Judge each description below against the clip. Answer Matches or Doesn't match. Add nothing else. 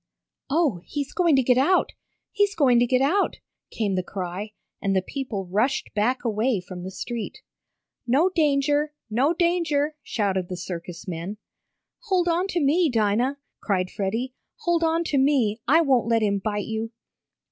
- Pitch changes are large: Matches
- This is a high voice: Matches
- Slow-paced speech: Doesn't match